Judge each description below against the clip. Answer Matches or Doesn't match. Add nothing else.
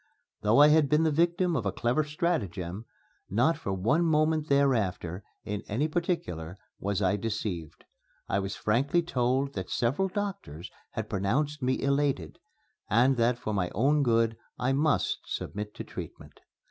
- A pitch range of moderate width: Doesn't match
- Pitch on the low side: Matches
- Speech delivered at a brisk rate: Doesn't match